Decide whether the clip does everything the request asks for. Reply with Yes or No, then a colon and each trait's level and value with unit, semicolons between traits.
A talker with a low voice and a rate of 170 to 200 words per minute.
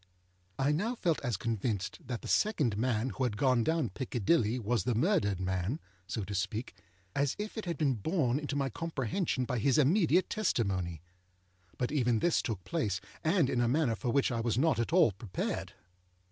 Yes: low, 125 Hz; average, 190 wpm